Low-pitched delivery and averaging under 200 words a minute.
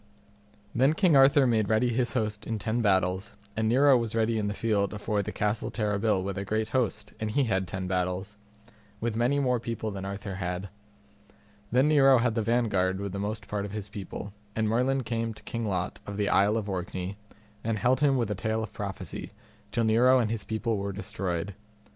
No: low, 110 Hz; fast, 205 wpm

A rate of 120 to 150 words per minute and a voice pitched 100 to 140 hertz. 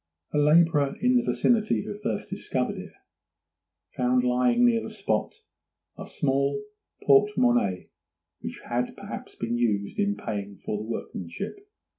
Yes: average, 140 wpm; low, 135 Hz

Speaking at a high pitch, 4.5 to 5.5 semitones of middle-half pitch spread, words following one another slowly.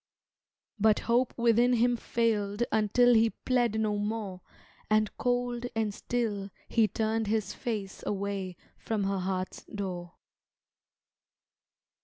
No: high, 215 Hz; average, 2.7 semitones; slow, 115 wpm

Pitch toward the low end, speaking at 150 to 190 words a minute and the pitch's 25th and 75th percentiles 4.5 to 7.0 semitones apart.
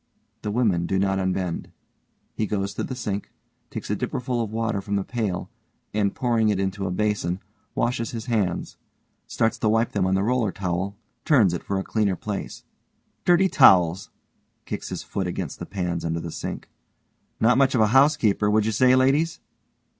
No: low, 105 Hz; average, 185 wpm; average, 3.5 semitones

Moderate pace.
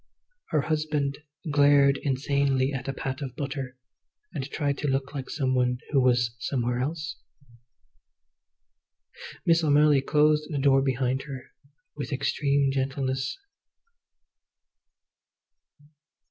No: slow, 110 wpm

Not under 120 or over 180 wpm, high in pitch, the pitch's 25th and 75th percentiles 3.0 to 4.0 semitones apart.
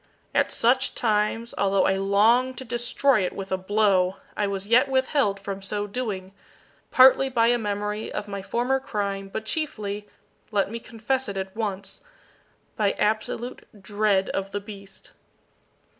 Yes: average, 155 wpm; high, 210 Hz; average, 3.3 semitones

